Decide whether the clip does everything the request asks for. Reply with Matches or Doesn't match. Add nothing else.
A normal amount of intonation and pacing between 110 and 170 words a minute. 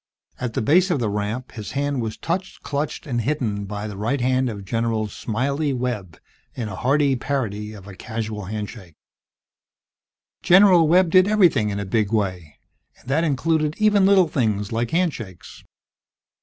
Doesn't match